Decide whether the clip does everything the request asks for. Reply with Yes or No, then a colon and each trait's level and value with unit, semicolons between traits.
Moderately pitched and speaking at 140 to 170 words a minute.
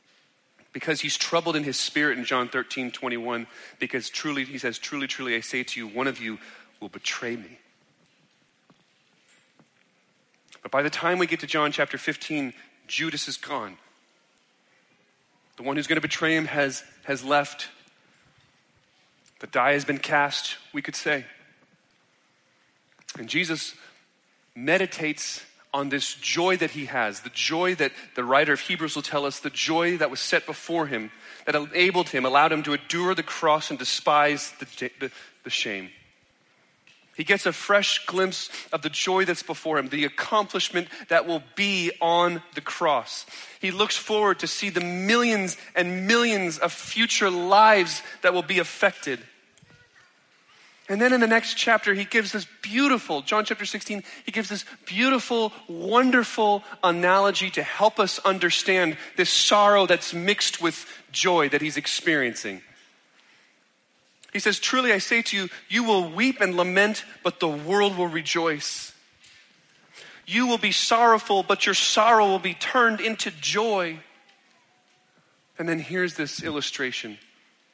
Yes: medium, 175 Hz; average, 155 wpm